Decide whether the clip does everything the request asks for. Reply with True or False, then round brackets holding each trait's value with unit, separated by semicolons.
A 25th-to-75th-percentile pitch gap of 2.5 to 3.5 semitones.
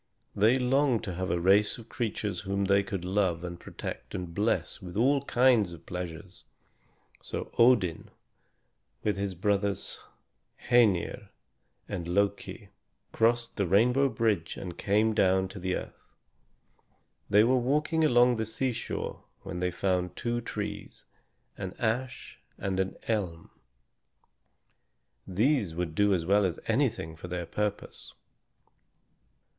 False (4.3 semitones)